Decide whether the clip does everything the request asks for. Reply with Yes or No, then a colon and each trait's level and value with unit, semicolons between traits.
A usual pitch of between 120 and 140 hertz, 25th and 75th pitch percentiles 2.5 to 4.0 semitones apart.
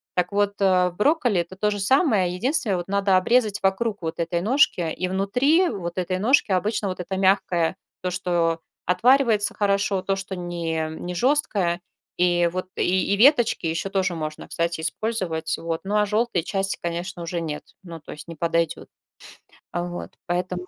No: medium, 185 Hz; average, 3.1 semitones